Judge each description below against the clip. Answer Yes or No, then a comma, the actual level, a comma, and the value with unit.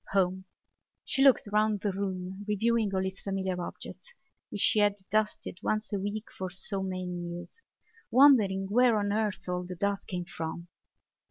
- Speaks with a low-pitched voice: No, high, 195 Hz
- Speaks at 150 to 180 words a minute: Yes, average, 165 wpm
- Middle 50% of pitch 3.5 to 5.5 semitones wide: No, narrow, 2.5 semitones